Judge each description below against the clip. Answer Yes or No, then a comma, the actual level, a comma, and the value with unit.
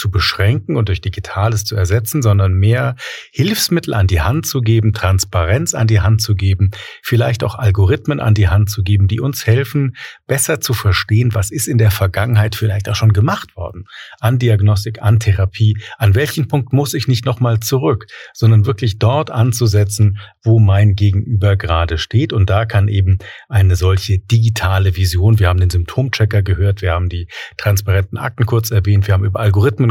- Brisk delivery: No, average, 180 wpm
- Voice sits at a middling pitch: No, low, 105 Hz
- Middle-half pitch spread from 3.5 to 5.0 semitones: No, average, 3.0 semitones